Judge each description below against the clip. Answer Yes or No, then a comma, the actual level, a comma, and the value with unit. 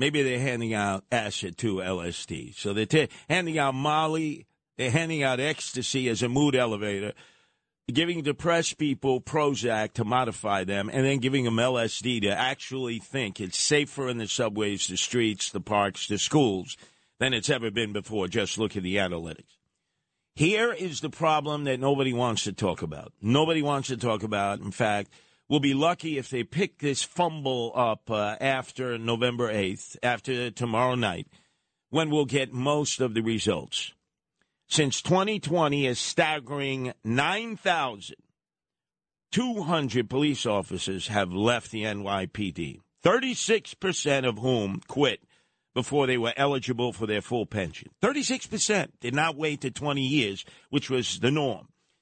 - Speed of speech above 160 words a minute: No, average, 150 wpm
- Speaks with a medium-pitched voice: No, low, 125 Hz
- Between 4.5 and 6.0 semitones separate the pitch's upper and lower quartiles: Yes, wide, 5.4 semitones